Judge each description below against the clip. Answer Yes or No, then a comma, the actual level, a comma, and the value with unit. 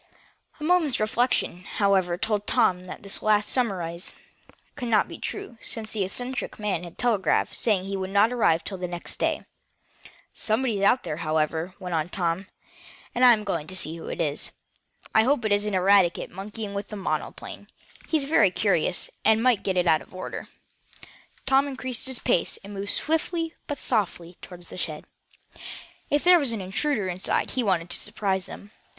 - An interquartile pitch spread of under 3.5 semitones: No, average, 4.9 semitones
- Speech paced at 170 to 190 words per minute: Yes, average, 180 wpm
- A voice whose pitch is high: Yes, high, 200 Hz